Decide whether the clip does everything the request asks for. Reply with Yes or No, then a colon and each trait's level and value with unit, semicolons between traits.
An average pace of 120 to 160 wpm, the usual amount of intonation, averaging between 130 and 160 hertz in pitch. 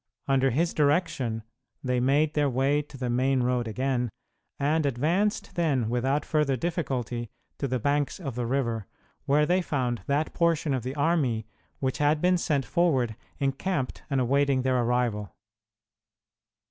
Yes: average, 150 wpm; average, 3.3 semitones; low, 135 Hz